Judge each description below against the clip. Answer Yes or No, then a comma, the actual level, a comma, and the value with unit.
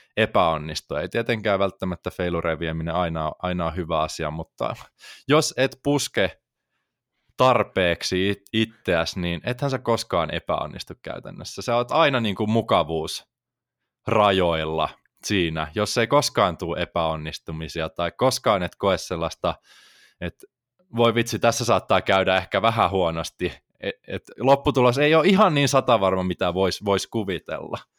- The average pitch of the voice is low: Yes, very low, 95 Hz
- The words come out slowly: No, average, 130 wpm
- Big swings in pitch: Yes, wide, 5.8 semitones